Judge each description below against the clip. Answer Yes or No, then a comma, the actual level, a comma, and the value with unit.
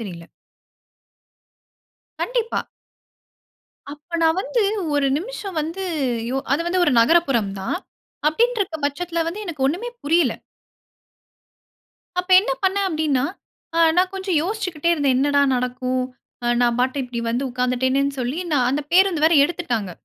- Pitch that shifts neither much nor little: No, wide, 5.8 semitones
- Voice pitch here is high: Yes, very high, 305 Hz